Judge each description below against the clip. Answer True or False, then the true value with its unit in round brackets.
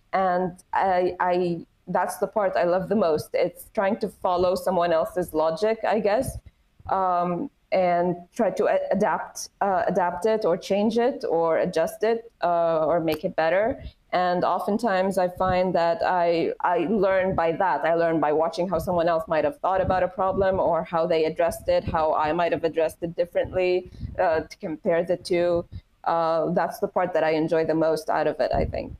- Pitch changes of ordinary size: False (2.2 semitones)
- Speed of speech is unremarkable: True (190 wpm)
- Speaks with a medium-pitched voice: True (175 Hz)